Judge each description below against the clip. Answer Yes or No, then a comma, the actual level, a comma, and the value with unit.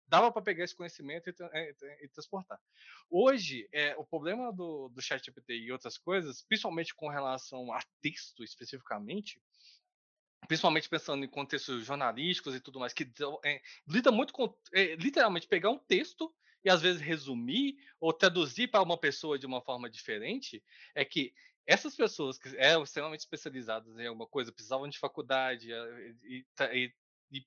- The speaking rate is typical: Yes, average, 165 wpm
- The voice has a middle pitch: Yes, medium, 155 Hz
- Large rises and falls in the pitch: Yes, wide, 8.1 semitones